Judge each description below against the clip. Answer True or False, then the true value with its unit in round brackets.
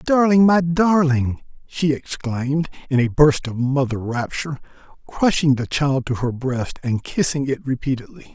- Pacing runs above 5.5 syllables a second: False (4.5 syllables/s)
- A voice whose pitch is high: False (140 Hz)